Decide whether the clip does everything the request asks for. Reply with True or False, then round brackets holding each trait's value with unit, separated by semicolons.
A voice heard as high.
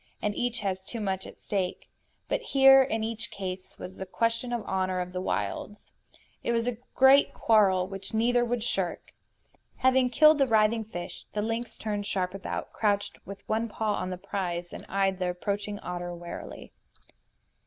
True (205 Hz)